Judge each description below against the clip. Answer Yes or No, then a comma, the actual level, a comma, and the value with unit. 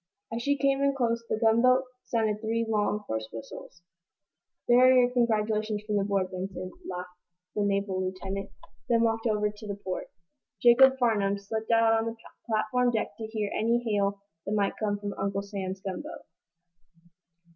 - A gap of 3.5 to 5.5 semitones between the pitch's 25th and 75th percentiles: No, average, 2.7 semitones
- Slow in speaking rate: No, average, 165 wpm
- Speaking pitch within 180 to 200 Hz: No, high, 215 Hz